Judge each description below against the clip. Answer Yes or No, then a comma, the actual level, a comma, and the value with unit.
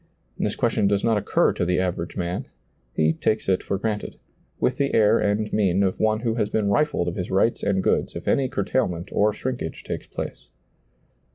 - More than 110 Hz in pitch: No, low, 105 Hz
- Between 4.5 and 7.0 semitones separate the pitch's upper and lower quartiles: No, average, 3.2 semitones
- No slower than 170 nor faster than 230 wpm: Yes, average, 195 wpm